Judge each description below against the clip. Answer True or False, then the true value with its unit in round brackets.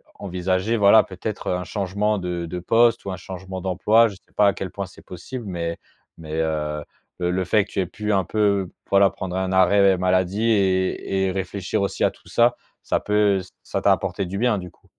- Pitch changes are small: True (2.2 semitones)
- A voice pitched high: False (95 Hz)